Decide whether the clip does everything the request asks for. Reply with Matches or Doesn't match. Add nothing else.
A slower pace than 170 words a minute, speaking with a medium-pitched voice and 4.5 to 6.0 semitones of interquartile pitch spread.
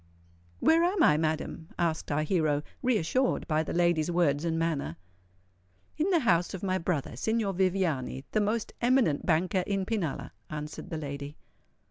Matches